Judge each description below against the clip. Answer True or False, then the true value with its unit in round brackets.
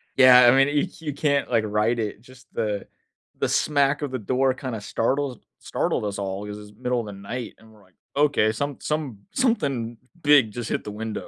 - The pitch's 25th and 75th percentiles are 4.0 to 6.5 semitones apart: True (4.6 semitones)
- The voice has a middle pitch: False (125 Hz)